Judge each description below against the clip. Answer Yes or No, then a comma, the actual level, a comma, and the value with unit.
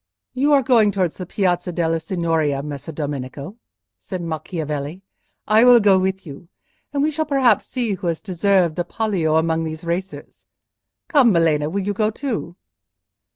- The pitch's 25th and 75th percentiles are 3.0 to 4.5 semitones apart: No, average, 4.9 semitones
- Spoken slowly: No, average, 160 wpm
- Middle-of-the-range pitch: Yes, medium, 180 Hz